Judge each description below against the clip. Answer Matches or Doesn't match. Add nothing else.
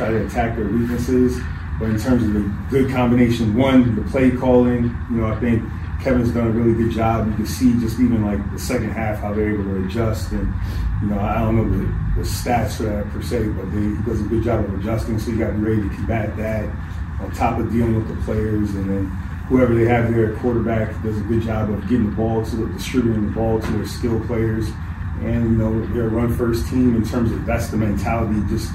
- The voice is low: Matches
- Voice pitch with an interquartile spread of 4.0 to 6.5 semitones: Doesn't match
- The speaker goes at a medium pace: Doesn't match